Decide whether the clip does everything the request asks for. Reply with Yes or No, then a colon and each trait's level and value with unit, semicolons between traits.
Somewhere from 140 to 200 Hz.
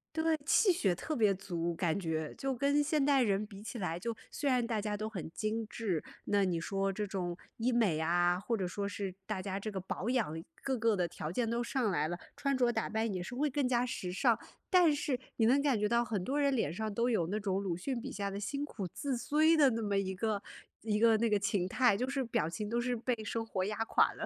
No: high, 215 Hz